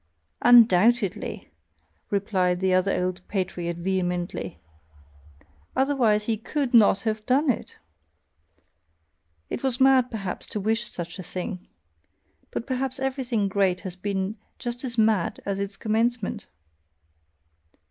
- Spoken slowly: Yes, slow, 115 wpm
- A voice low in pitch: No, high, 210 Hz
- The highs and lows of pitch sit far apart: No, average, 4.5 semitones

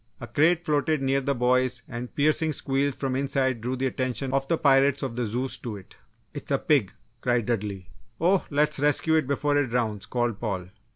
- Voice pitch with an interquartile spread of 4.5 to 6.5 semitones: No, average, 3.1 semitones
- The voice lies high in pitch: No, low, 130 Hz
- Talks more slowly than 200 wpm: No, fast, 205 wpm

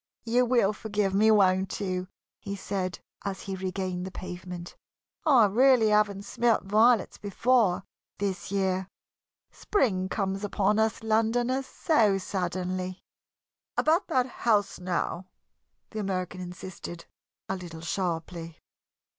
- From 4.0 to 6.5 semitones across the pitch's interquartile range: No, average, 3.1 semitones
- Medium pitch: No, high, 195 Hz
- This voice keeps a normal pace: No, slow, 120 wpm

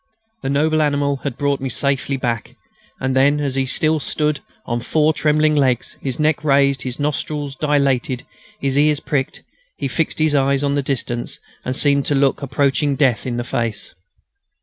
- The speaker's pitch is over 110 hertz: Yes, medium, 140 Hz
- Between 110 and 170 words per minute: No, average, 180 wpm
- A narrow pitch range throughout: Yes, narrow, 1.8 semitones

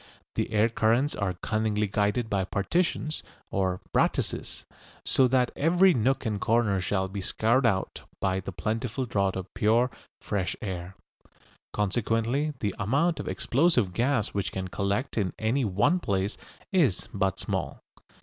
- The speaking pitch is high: No, low, 110 Hz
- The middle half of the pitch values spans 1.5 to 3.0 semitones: No, average, 4.4 semitones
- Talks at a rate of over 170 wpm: No, average, 145 wpm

